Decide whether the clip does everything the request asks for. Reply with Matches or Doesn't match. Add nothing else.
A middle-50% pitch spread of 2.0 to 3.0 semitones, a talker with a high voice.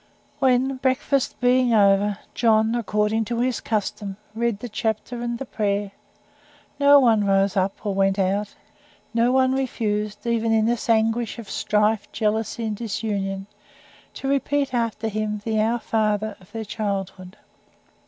Matches